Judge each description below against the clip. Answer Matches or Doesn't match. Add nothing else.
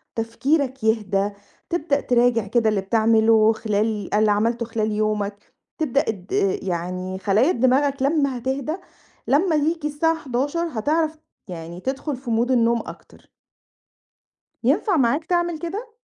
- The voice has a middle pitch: Doesn't match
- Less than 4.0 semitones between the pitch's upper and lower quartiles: Doesn't match